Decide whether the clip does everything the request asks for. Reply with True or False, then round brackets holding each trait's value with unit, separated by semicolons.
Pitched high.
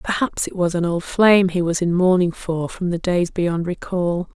False (175 Hz)